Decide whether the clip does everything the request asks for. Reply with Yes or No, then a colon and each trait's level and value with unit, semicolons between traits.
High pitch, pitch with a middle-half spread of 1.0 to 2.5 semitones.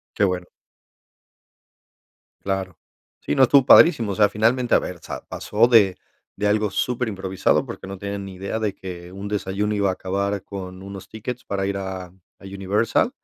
No: low, 100 Hz; narrow, 2.0 semitones